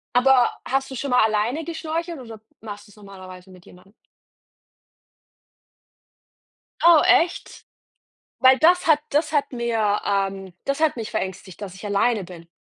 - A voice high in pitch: Yes, high, 225 Hz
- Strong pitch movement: Yes, wide, 6.3 semitones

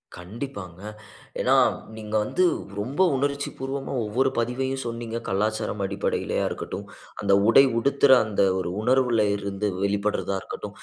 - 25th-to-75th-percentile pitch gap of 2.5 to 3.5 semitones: No, average, 4.5 semitones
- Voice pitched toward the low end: Yes, low, 115 Hz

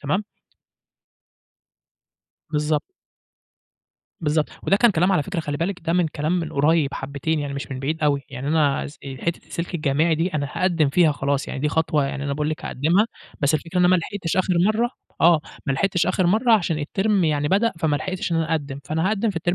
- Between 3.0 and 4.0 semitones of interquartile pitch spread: Yes, average, 3.7 semitones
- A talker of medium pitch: Yes, medium, 160 Hz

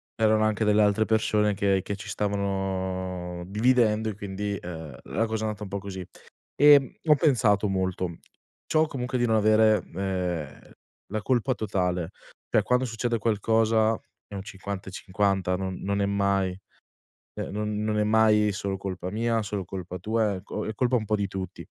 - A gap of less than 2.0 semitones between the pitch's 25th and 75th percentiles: No, narrow, 2.4 semitones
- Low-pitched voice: Yes, low, 105 Hz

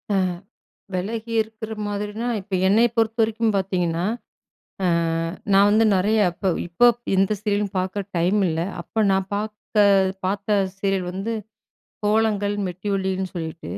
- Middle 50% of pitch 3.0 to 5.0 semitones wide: No, narrow, 2.6 semitones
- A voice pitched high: Yes, high, 205 Hz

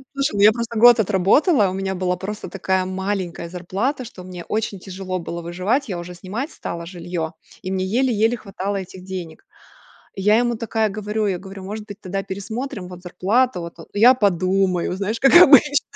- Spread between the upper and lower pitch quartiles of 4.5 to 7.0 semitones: No, average, 3.3 semitones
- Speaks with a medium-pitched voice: No, high, 195 Hz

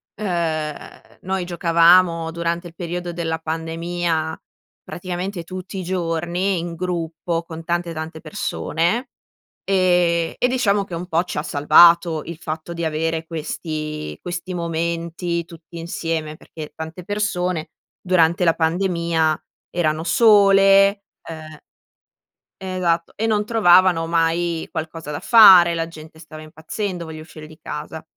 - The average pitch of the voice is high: No, medium, 170 Hz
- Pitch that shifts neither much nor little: No, narrow, 1.8 semitones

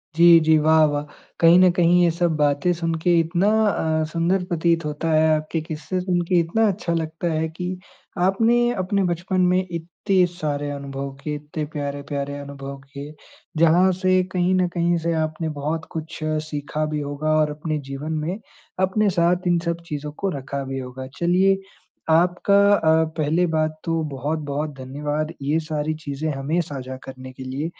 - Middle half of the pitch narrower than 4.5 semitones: Yes, average, 3.0 semitones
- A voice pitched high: No, medium, 160 Hz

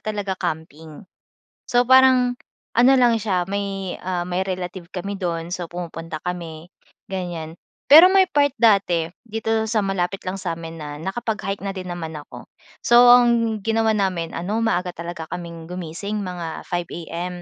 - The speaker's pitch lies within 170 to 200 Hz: Yes, medium, 185 Hz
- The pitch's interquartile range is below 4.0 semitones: No, average, 4.5 semitones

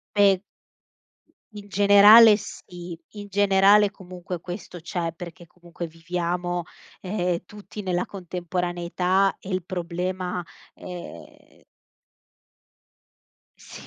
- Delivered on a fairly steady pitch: Yes, narrow, 2.1 semitones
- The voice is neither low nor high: Yes, medium, 180 Hz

